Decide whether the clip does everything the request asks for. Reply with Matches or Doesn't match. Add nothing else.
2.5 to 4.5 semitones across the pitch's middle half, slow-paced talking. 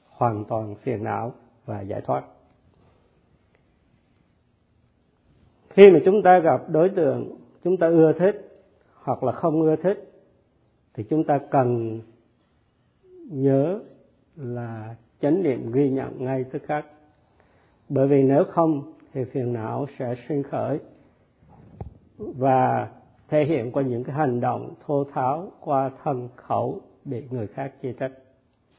Matches